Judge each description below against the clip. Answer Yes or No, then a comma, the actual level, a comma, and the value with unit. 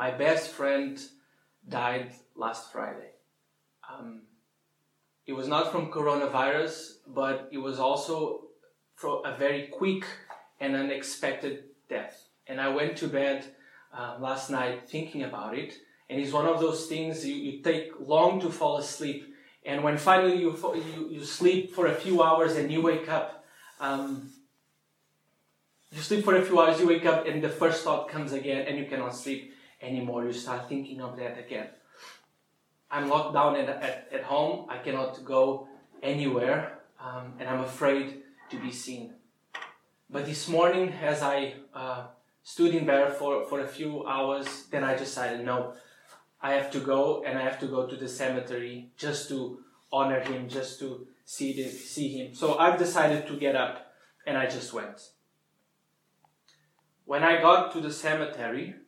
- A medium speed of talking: Yes, average, 165 wpm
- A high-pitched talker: No, medium, 140 Hz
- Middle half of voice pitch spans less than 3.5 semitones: Yes, average, 3.1 semitones